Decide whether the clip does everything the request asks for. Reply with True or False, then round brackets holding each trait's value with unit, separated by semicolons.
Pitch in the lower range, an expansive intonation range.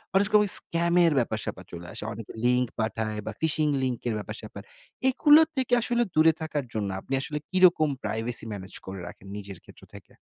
True (125 Hz; 8.1 semitones)